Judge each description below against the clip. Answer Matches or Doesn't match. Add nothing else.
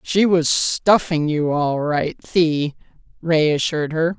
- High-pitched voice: Doesn't match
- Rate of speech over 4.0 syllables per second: Doesn't match